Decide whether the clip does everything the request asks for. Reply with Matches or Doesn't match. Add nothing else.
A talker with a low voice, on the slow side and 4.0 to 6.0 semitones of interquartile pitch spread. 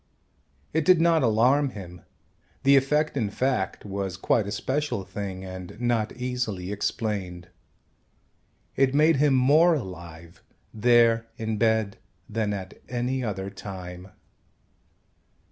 Matches